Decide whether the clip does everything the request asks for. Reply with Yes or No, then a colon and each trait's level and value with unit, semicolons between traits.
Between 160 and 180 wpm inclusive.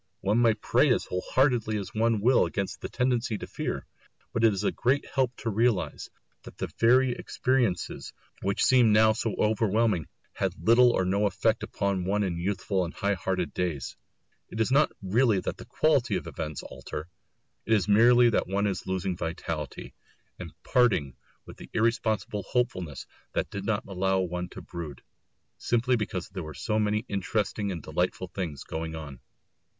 Yes: average, 175 wpm